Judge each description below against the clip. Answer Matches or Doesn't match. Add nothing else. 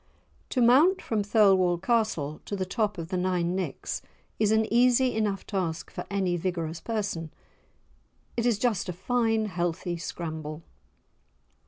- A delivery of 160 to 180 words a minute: Doesn't match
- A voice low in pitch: Doesn't match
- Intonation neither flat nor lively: Matches